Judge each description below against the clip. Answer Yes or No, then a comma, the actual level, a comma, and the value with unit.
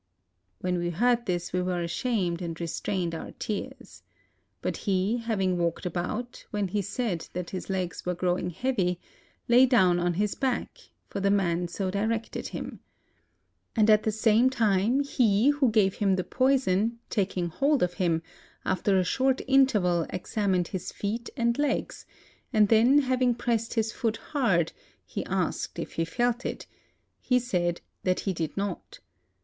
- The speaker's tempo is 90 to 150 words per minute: No, average, 165 wpm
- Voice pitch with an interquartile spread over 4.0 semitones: Yes, average, 4.9 semitones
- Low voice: No, high, 200 Hz